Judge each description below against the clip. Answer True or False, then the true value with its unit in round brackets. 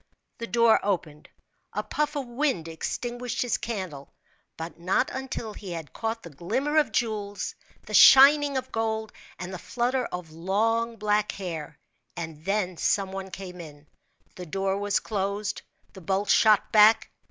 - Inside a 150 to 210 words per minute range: True (155 wpm)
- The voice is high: True (205 Hz)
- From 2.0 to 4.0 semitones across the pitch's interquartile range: False (4.4 semitones)